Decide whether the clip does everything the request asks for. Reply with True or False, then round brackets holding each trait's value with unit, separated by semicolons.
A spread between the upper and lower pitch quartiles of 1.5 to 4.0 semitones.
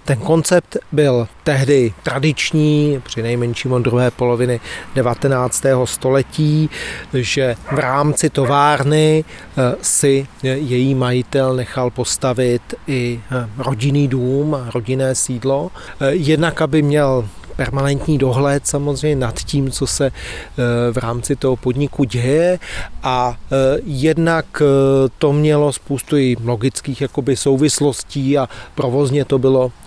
True (2.5 semitones)